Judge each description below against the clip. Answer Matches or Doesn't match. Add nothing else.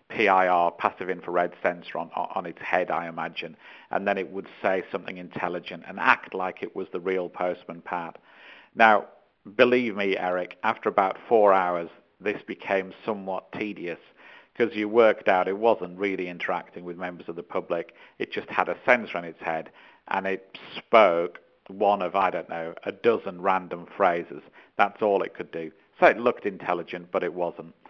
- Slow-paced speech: Doesn't match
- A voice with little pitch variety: Matches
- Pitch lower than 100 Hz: Matches